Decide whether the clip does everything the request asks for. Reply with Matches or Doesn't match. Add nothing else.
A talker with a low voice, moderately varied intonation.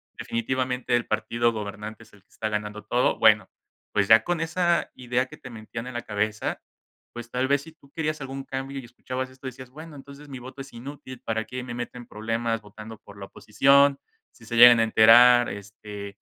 Matches